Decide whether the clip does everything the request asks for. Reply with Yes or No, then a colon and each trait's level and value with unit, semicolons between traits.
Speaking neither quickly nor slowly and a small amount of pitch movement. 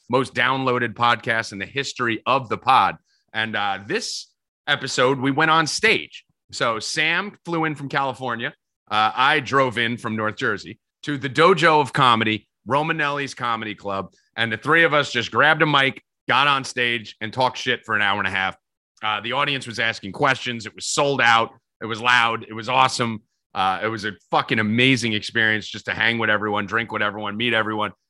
No: average, 195 wpm; average, 3.9 semitones